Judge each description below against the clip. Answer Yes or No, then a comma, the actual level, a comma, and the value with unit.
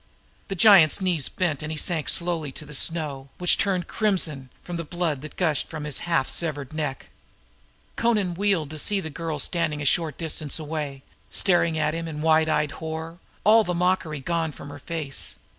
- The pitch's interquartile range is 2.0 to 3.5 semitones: Yes, average, 2.7 semitones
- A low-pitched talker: No, medium, 160 Hz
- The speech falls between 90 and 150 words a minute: No, average, 175 wpm